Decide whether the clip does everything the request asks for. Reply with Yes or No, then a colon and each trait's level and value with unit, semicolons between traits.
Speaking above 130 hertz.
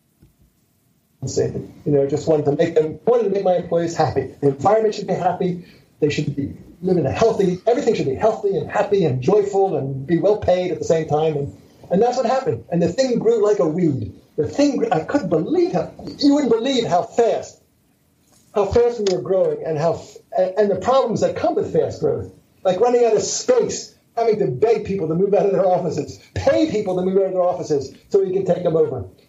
Yes: high, 190 Hz